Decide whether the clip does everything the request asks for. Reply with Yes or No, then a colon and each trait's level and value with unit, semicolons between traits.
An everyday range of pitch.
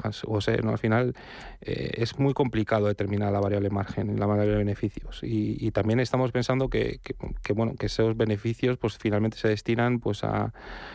No: narrow, 1.9 semitones